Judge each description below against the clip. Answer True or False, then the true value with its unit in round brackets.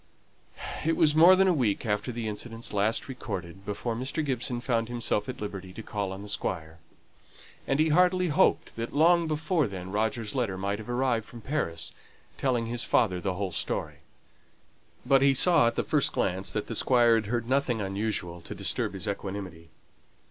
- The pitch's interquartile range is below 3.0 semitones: False (5.1 semitones)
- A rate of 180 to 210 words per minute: True (185 wpm)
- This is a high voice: False (115 Hz)